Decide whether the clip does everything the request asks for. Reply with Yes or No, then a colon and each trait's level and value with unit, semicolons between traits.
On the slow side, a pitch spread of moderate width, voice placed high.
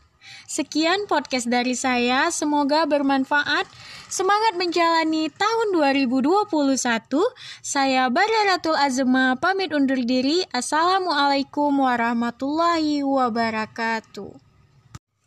Yes: slow, 75 wpm; average, 4.8 semitones; very high, 285 Hz